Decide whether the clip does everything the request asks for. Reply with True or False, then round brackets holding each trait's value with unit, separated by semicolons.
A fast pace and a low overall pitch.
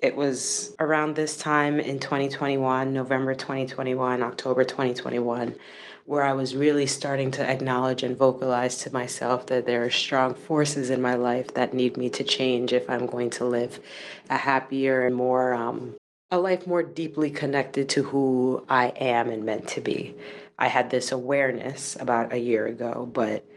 False (170 wpm; 130 Hz)